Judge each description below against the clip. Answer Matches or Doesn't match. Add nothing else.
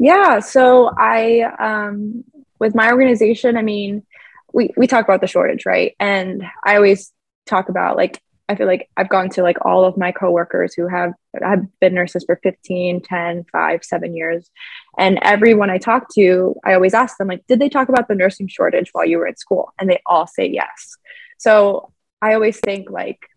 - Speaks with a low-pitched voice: Doesn't match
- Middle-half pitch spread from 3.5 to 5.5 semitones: Matches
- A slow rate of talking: Doesn't match